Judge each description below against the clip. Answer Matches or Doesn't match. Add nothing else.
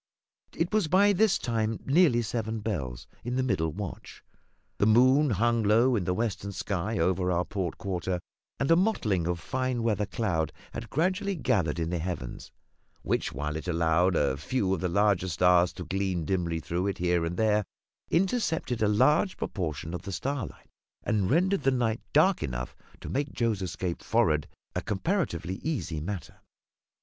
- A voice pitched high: Doesn't match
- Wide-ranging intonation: Matches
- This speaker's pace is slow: Doesn't match